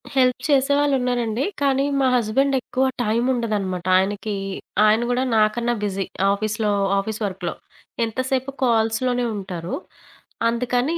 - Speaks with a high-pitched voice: Yes, high, 235 Hz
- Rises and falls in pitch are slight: No, average, 3.5 semitones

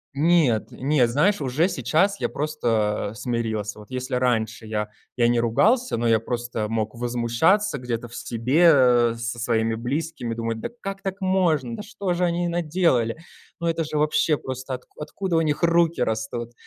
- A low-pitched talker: Yes, low, 125 Hz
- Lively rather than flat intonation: Yes, wide, 6.2 semitones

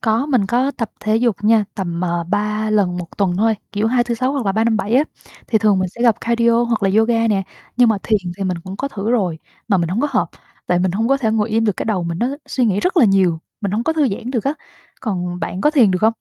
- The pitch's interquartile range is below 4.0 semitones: Yes, average, 3.6 semitones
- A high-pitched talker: Yes, high, 215 Hz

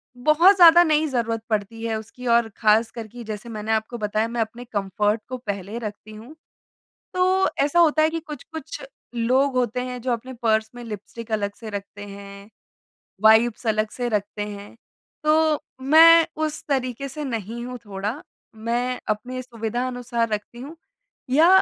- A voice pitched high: Yes, high, 235 Hz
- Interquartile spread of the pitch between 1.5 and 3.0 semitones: No, average, 3.5 semitones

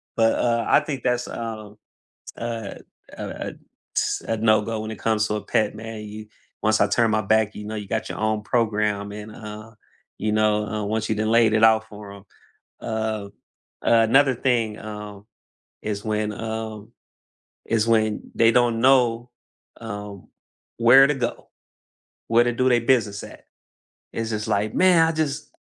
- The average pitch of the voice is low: Yes, low, 110 Hz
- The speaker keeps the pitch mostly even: Yes, narrow, 1.5 semitones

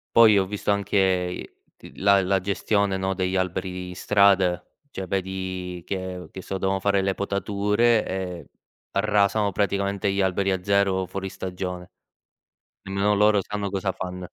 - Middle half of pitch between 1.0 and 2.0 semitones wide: Yes, narrow, 1.3 semitones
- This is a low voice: Yes, very low, 95 Hz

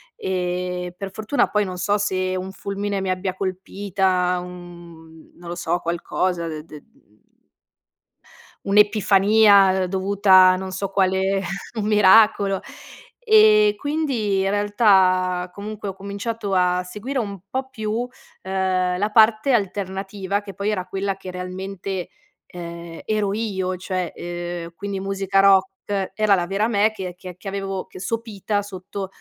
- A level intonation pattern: Yes, narrow, 2.0 semitones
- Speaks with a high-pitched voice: Yes, high, 195 Hz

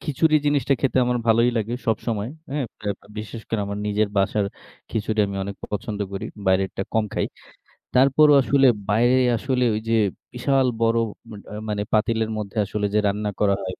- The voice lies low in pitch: Yes, low, 110 Hz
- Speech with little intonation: No, average, 3.4 semitones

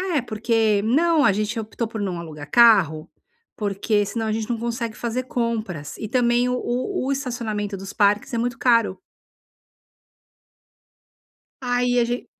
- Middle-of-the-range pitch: No, high, 230 Hz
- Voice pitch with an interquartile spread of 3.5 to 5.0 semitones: No, average, 2.9 semitones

